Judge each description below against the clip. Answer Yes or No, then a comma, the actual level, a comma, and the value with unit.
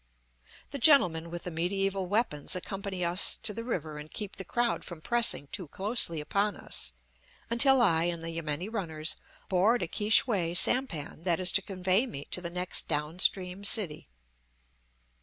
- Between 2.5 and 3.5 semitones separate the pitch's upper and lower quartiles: No, average, 3.9 semitones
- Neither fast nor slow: Yes, average, 170 wpm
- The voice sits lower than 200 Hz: Yes, medium, 185 Hz